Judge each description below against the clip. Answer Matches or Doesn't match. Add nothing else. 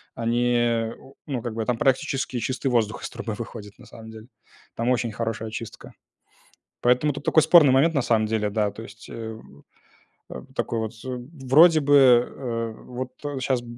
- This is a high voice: Doesn't match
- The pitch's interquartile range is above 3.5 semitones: Doesn't match